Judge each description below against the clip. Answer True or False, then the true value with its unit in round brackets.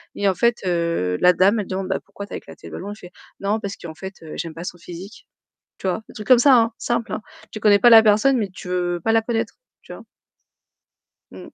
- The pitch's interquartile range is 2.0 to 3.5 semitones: False (3.9 semitones)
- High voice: True (200 Hz)